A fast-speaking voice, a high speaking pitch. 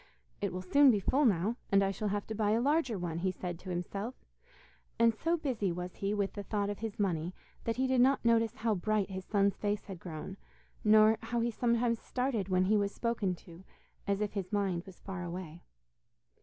Yes: fast, 215 wpm; high, 205 Hz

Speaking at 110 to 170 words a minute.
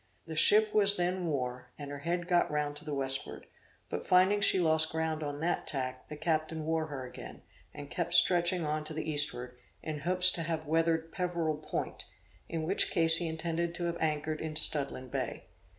No: average, 195 wpm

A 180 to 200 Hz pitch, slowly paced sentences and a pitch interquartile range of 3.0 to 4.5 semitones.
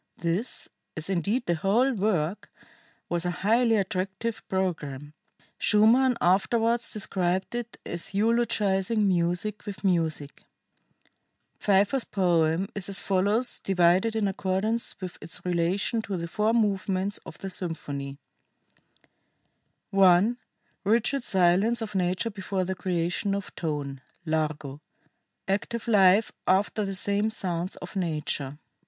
Yes: high, 190 Hz; slow, 120 wpm; average, 3.5 semitones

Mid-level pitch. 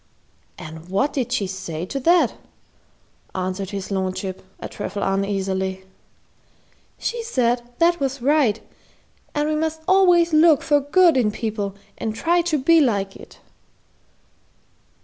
No: high, 240 Hz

